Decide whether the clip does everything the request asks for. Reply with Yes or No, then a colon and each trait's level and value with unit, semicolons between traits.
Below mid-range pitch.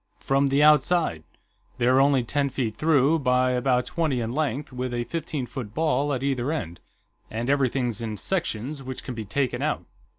Yes: low, 130 Hz